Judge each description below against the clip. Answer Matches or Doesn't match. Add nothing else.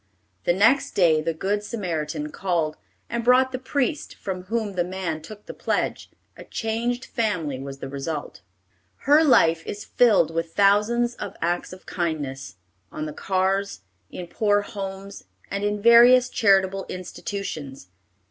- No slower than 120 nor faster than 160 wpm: Matches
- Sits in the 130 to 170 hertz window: Doesn't match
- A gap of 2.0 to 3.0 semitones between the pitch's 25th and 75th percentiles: Doesn't match